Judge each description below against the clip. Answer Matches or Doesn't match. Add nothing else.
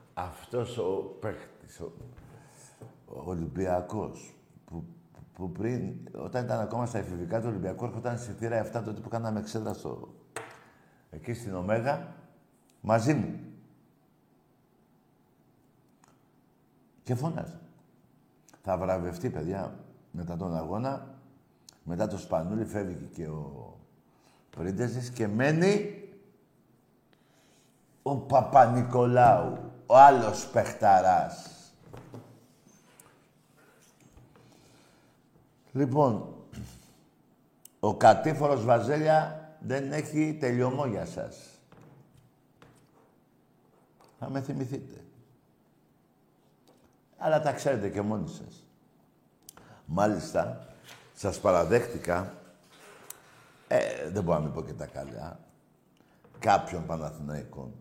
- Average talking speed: Doesn't match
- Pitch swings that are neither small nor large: Doesn't match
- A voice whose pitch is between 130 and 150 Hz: Doesn't match